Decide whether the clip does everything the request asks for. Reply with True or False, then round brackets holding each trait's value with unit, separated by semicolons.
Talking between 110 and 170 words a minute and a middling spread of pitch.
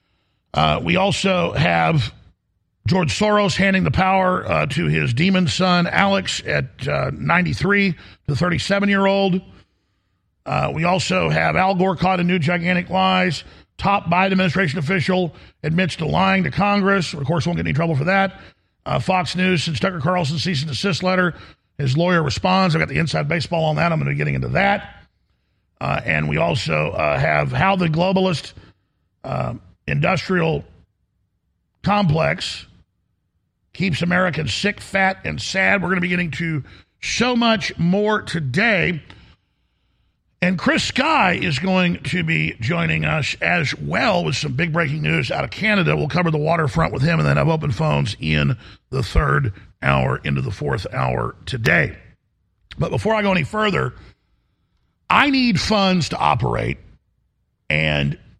False (160 wpm; 6.6 semitones)